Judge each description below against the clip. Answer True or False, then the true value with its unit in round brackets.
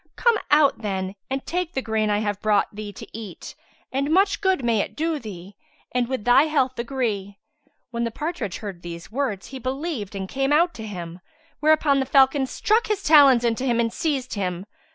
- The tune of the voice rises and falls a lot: True (6.0 semitones)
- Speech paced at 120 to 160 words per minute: False (195 wpm)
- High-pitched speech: True (245 Hz)